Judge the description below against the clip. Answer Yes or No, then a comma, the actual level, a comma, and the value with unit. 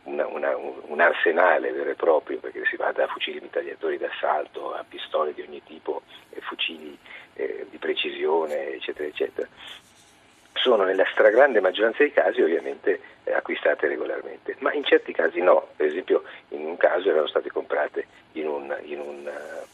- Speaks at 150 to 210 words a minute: Yes, average, 160 wpm